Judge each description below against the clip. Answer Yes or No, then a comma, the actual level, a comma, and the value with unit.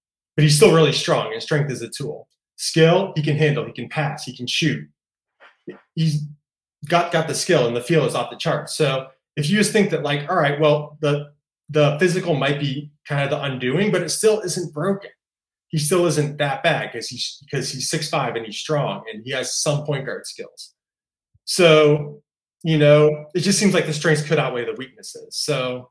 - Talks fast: Yes, fast, 210 wpm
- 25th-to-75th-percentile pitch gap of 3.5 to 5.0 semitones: No, average, 2.9 semitones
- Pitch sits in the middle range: Yes, medium, 150 Hz